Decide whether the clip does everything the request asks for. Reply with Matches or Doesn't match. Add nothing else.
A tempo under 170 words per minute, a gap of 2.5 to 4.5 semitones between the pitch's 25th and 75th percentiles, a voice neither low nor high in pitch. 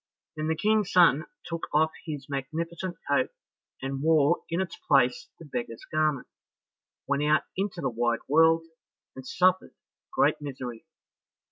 Matches